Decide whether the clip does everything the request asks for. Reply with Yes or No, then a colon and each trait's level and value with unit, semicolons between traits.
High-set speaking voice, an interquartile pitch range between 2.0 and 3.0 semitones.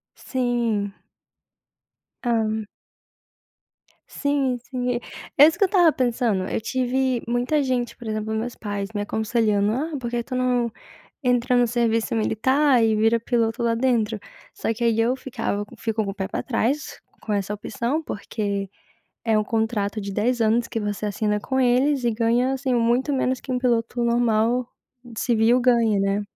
Yes: high, 235 Hz; narrow, 2.5 semitones